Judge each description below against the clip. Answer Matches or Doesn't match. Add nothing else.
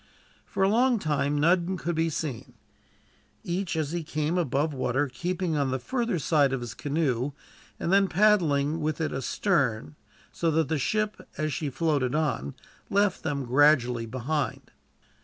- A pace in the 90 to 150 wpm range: Doesn't match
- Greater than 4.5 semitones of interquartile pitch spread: Doesn't match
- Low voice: Doesn't match